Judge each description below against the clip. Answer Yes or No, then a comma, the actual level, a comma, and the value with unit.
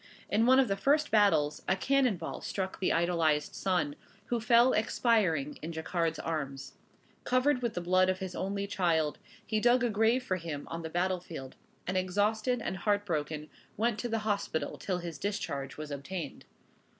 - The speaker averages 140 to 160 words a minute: No, average, 180 wpm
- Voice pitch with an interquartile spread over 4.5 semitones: Yes, wide, 5.5 semitones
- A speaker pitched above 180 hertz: Yes, high, 190 Hz